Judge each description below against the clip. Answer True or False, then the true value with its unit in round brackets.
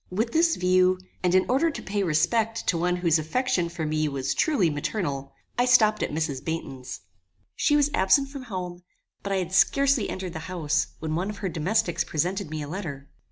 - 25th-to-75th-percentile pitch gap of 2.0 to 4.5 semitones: False (5.4 semitones)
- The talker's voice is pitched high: False (180 Hz)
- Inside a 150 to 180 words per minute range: False (200 wpm)